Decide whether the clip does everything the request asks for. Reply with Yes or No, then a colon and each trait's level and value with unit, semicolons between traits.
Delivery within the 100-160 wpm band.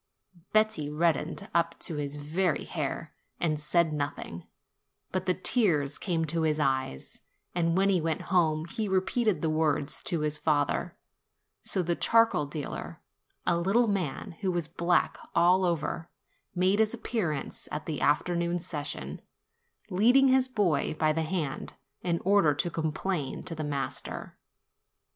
Yes: average, 150 wpm